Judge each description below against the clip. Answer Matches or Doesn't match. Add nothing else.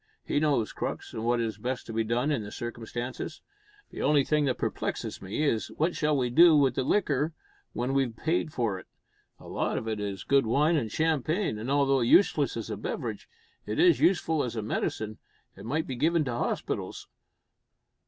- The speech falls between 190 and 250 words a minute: Matches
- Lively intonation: Doesn't match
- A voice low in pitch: Matches